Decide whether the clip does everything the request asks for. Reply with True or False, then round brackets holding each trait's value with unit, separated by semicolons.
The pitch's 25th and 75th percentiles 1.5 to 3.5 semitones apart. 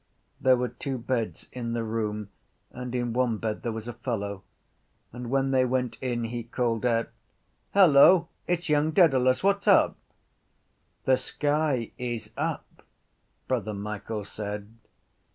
True (2.8 semitones)